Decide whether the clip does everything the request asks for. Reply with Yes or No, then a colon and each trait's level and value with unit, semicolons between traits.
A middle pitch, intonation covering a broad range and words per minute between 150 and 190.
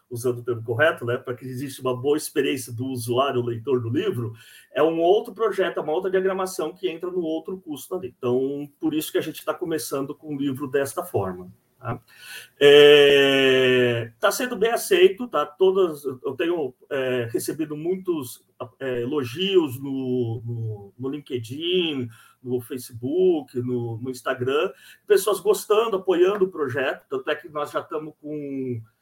Yes: medium, 145 Hz; wide, 7.1 semitones; average, 165 wpm